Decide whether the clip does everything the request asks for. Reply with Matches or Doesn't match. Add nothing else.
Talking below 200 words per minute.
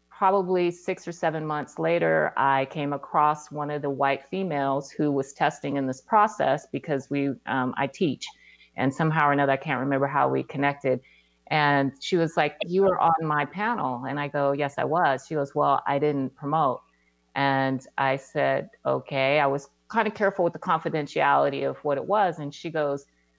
Matches